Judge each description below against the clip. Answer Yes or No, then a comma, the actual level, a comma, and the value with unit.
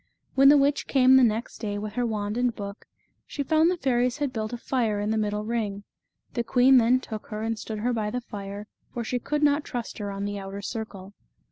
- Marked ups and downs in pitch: No, average, 3.5 semitones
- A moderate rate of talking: No, fast, 235 wpm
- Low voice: No, high, 225 Hz